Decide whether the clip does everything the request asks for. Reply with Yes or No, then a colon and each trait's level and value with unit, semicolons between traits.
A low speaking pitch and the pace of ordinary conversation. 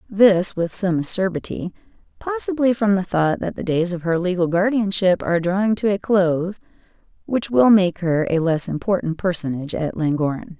No: high, 190 Hz; average, 165 wpm